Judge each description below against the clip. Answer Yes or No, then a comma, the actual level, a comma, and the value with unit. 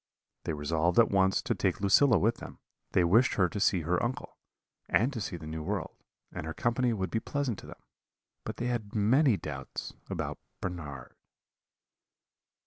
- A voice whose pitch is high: No, low, 100 Hz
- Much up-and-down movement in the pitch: Yes, wide, 6.2 semitones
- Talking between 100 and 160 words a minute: No, average, 175 wpm